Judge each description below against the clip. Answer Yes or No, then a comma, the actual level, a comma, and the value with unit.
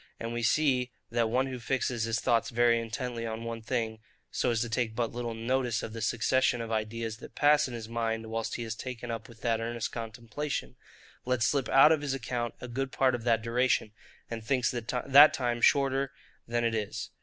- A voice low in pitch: Yes, low, 120 Hz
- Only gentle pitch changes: Yes, narrow, 2.0 semitones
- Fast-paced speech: Yes, fast, 210 wpm